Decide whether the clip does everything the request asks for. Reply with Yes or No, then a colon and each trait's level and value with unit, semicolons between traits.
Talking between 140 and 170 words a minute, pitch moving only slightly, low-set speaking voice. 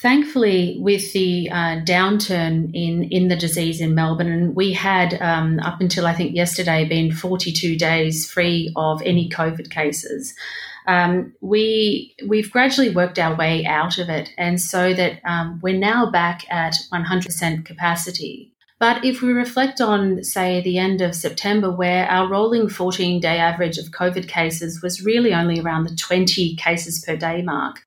No: average, 165 wpm; narrow, 2.0 semitones; medium, 175 Hz